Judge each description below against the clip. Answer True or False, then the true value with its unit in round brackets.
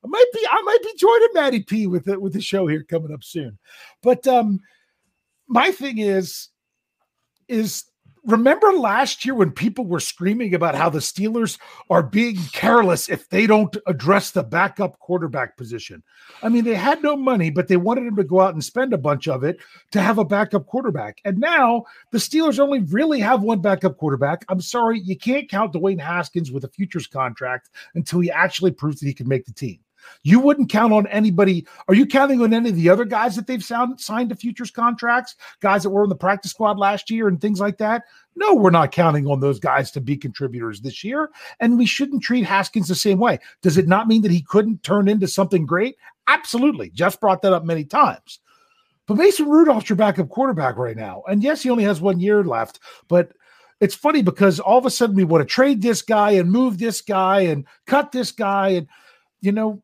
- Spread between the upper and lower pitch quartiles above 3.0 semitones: True (5.1 semitones)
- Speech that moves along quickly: True (215 wpm)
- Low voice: False (200 Hz)